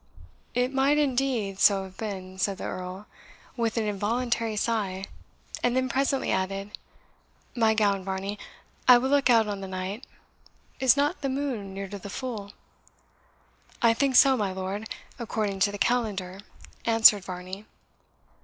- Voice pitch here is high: Yes, high, 210 Hz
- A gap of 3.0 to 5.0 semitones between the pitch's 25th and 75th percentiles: Yes, average, 4.2 semitones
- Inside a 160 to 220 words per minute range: No, average, 150 wpm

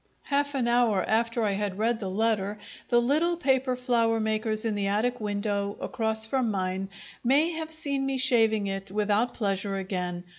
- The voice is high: Yes, high, 220 Hz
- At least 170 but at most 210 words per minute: Yes, average, 175 wpm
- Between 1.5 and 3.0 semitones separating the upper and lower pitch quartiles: No, average, 3.8 semitones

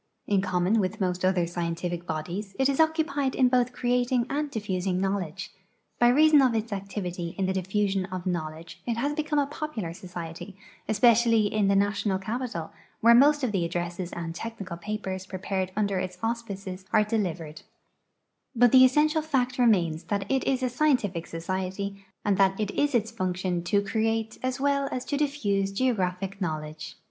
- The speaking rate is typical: Yes, average, 170 wpm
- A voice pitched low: No, high, 200 Hz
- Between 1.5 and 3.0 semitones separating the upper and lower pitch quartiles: No, average, 5.2 semitones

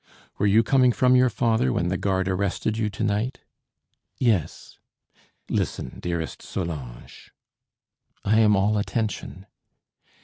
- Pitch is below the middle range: Yes, low, 105 Hz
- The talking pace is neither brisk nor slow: No, slow, 125 wpm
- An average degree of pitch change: Yes, average, 3.4 semitones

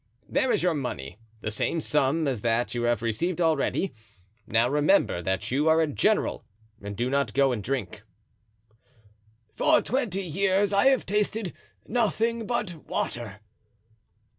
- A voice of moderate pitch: Yes, medium, 145 Hz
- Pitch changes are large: Yes, wide, 8.6 semitones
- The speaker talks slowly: No, average, 145 wpm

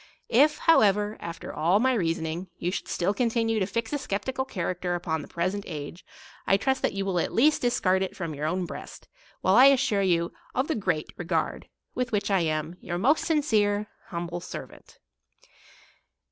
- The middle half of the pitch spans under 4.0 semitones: No, average, 5.1 semitones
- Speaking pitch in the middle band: No, high, 195 Hz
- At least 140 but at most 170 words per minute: No, average, 185 wpm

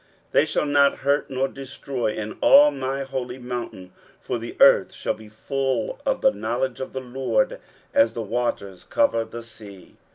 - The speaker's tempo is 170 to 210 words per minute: Yes, average, 175 wpm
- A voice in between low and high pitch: No, low, 130 Hz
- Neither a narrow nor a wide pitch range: Yes, average, 3.5 semitones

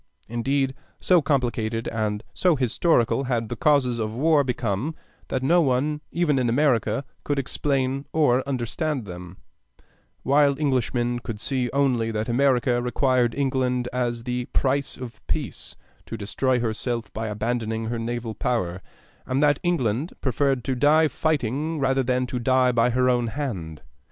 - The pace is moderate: Yes, average, 150 wpm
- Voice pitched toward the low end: Yes, low, 125 Hz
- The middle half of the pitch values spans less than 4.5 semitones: Yes, average, 3.2 semitones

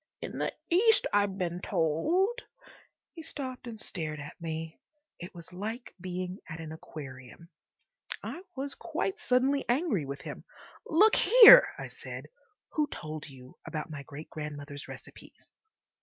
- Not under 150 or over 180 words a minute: No, average, 140 wpm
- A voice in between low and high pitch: Yes, medium, 180 Hz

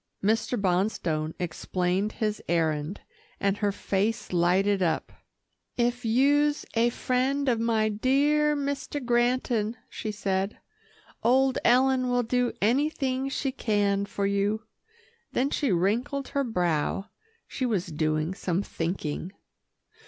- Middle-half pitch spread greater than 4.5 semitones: Yes, average, 5.1 semitones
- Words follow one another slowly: Yes, slow, 120 wpm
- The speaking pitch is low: No, high, 220 Hz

